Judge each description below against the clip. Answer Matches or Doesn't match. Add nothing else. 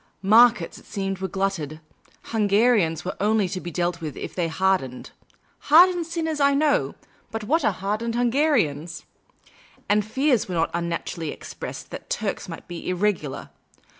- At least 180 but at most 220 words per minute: Doesn't match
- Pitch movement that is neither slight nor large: Doesn't match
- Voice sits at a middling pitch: Doesn't match